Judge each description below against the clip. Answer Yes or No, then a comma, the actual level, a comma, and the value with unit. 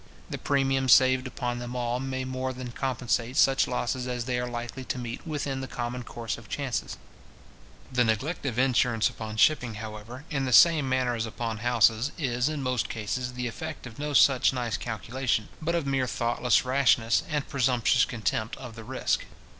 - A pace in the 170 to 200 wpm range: Yes, average, 190 wpm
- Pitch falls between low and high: No, low, 125 Hz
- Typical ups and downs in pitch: No, narrow, 2.1 semitones